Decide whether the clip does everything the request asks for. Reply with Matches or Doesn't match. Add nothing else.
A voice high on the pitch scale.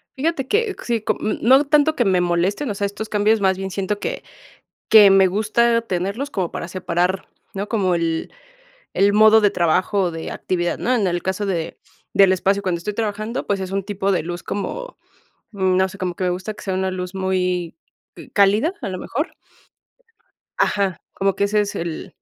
Matches